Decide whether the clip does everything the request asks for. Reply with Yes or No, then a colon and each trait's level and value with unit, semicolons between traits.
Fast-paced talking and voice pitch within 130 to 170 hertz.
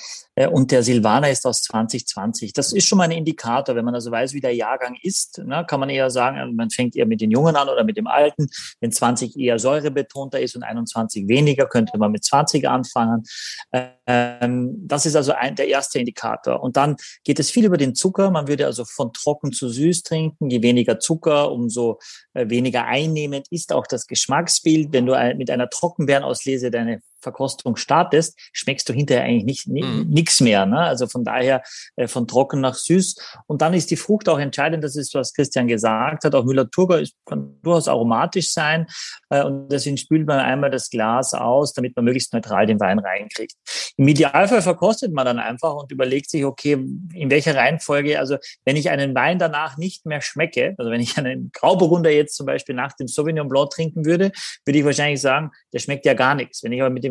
Yes: fast, 200 wpm; medium, 140 Hz